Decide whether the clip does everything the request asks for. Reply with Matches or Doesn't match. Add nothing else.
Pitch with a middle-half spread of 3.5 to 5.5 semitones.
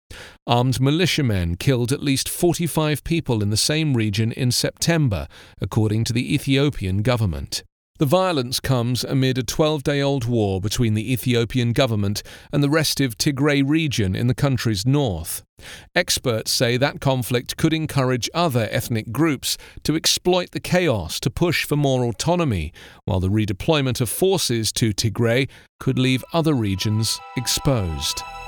Matches